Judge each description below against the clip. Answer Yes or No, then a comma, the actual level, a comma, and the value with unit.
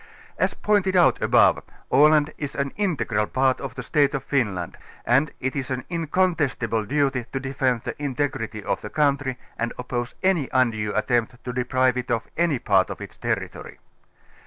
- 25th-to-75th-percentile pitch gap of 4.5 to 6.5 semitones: No, average, 3.4 semitones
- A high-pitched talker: No, low, 130 Hz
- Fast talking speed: No, average, 170 wpm